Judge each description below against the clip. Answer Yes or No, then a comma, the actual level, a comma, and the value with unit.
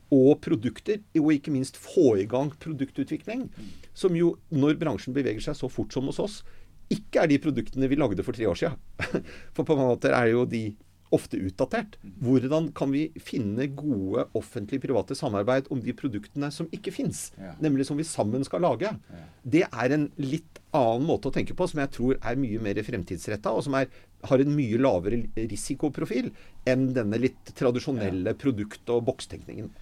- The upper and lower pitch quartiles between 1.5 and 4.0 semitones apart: No, average, 4.5 semitones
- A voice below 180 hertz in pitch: Yes, low, 135 Hz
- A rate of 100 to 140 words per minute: No, average, 180 wpm